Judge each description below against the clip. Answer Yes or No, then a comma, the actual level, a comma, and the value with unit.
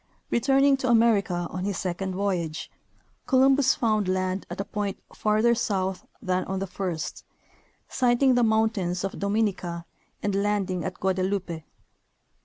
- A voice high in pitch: Yes, high, 200 Hz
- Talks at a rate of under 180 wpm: Yes, slow, 135 wpm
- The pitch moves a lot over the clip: No, average, 3.4 semitones